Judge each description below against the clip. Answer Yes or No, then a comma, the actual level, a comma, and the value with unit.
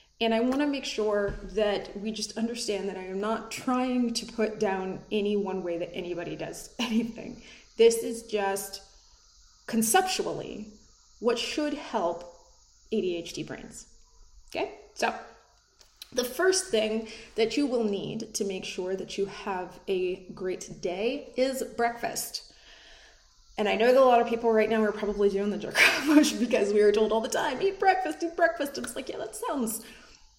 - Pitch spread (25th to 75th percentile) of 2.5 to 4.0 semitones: Yes, average, 3.4 semitones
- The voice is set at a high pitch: Yes, high, 220 Hz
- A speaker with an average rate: Yes, average, 170 wpm